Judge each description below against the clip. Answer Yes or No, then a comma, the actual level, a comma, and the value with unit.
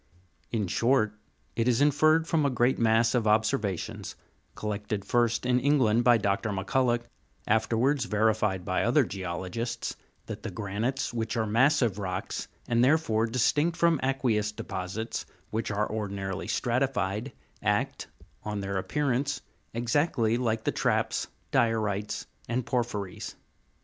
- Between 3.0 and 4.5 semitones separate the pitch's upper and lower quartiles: Yes, average, 3.3 semitones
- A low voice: Yes, low, 115 Hz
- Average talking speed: No, slow, 130 wpm